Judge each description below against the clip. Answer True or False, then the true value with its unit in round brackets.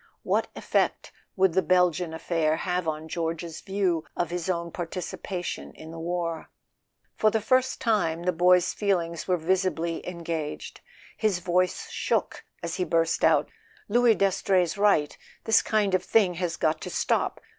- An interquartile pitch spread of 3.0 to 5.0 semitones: False (2.4 semitones)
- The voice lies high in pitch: False (175 Hz)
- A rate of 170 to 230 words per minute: False (160 wpm)